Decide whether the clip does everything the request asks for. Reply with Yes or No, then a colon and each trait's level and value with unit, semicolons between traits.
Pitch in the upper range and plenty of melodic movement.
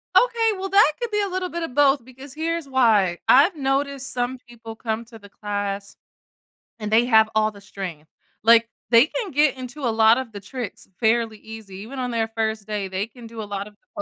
No: high, 230 Hz; average, 4.4 semitones